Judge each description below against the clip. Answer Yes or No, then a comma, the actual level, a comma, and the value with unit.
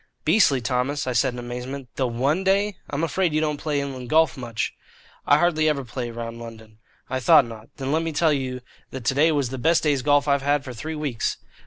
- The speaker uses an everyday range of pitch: Yes, average, 3.8 semitones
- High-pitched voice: No, medium, 140 Hz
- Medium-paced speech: No, fast, 220 wpm